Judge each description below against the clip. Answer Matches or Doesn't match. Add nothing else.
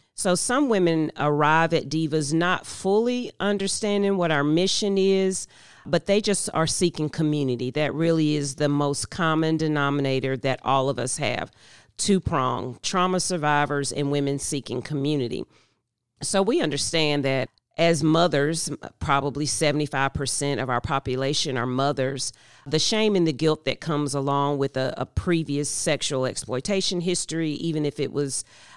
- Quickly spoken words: Doesn't match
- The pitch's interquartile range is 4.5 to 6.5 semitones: Doesn't match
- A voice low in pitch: Doesn't match